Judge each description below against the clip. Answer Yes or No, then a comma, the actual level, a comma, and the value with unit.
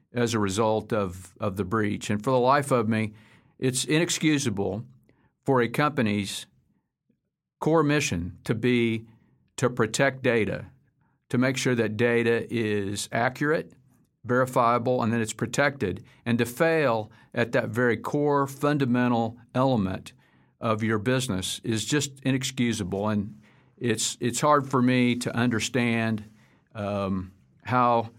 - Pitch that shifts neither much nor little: Yes, average, 3.0 semitones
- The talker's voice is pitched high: No, low, 120 Hz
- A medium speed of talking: No, slow, 130 wpm